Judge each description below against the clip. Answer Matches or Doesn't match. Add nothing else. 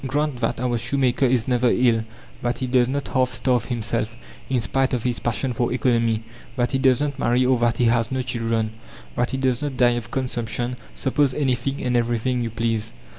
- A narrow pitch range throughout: Matches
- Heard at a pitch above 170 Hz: Doesn't match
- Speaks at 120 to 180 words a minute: Doesn't match